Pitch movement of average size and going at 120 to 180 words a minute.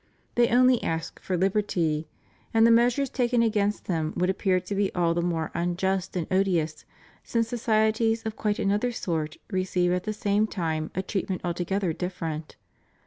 Yes: average, 4.1 semitones; average, 165 wpm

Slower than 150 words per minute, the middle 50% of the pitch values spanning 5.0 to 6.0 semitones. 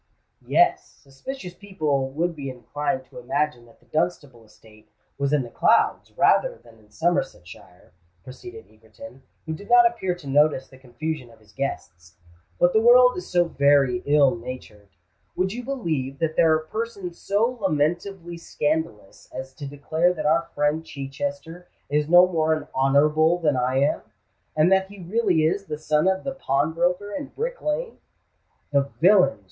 No: average, 165 wpm; wide, 5.6 semitones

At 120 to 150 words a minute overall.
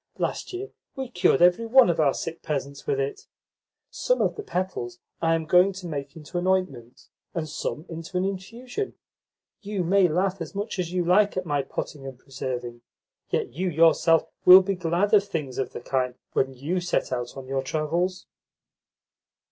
No: average, 185 wpm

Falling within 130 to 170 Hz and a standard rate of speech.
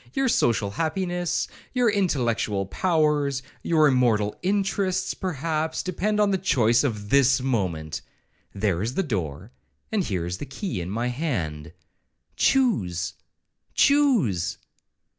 No: low, 135 Hz; slow, 105 wpm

